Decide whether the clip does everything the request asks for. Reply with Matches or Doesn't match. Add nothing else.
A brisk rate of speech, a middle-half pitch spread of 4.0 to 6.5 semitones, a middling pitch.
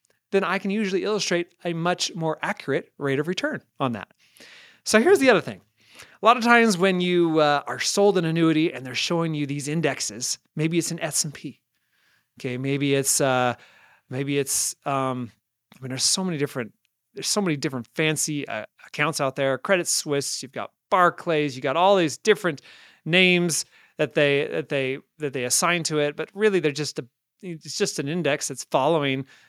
Doesn't match